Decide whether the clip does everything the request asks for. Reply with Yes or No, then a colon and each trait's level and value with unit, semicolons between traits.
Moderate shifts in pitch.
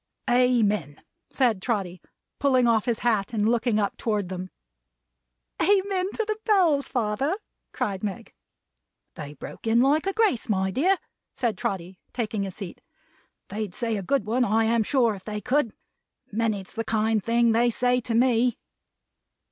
Yes: average, 3.5 semitones